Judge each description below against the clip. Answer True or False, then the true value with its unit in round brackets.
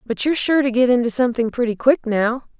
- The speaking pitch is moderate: False (245 Hz)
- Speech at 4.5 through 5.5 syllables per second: False (6.4 syllables/s)